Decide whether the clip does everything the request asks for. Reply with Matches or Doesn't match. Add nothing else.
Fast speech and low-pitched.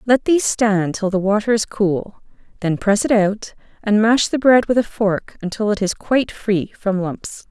Doesn't match